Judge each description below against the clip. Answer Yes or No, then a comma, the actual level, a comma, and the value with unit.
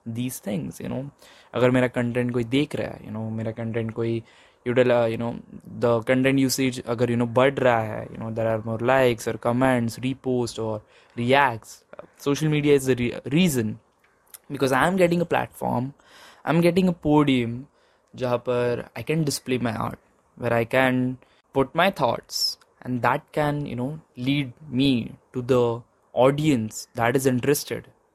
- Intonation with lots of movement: No, average, 2.8 semitones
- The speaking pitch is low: Yes, low, 125 Hz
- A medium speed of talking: Yes, average, 165 wpm